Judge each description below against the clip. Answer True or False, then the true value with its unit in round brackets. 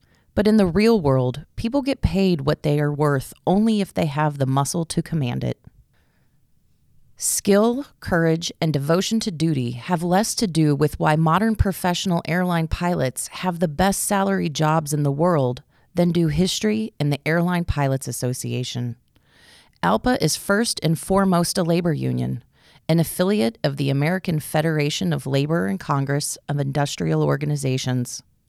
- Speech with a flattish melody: False (4.5 semitones)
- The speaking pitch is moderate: True (160 Hz)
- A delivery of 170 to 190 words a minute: False (155 wpm)